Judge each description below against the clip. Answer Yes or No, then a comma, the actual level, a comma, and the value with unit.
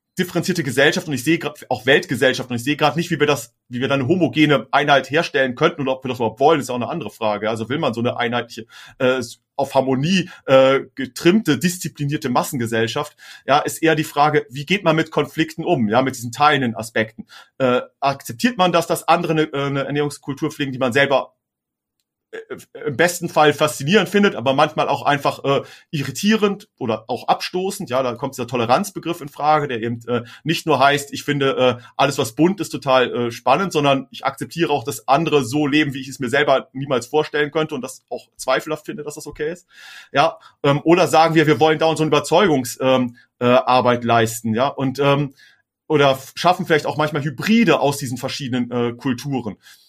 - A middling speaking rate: No, fast, 195 wpm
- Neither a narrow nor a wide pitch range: Yes, average, 3.3 semitones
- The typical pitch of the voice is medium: Yes, medium, 145 Hz